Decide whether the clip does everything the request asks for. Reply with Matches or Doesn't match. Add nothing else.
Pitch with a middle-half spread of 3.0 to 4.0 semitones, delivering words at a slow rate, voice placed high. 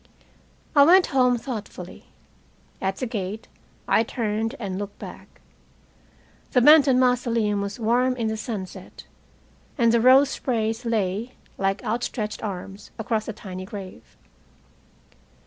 Matches